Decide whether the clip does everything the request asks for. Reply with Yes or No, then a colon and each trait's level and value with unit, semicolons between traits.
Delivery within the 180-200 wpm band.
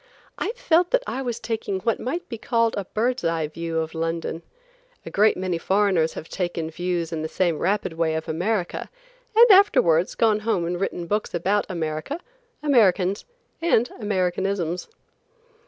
No: average, 160 wpm